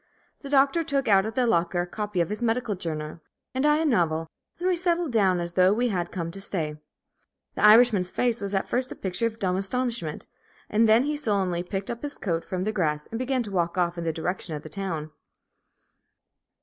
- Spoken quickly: Yes, fast, 220 wpm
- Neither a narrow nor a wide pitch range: No, wide, 5.8 semitones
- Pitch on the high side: Yes, high, 200 Hz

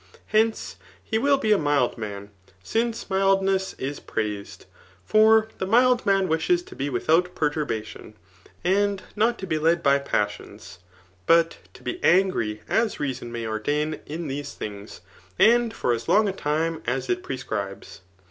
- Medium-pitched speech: Yes, medium, 160 Hz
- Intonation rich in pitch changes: Yes, wide, 8.4 semitones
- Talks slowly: No, average, 155 wpm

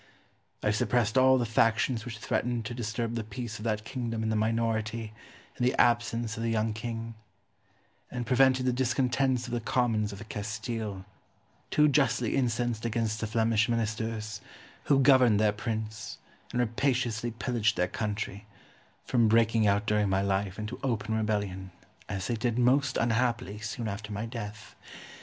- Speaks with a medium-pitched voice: No, low, 115 Hz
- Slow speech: No, average, 160 wpm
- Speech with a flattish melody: Yes, narrow, 2.1 semitones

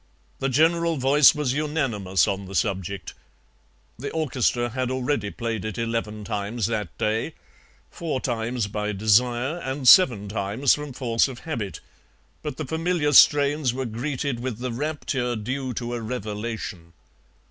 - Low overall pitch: Yes, low, 120 Hz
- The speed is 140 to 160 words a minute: Yes, average, 145 wpm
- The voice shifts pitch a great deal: No, average, 4.7 semitones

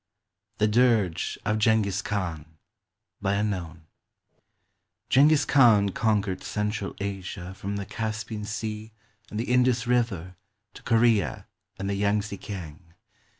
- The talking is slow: Yes, slow, 110 wpm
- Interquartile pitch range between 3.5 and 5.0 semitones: No, narrow, 2.5 semitones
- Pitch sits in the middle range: No, low, 105 Hz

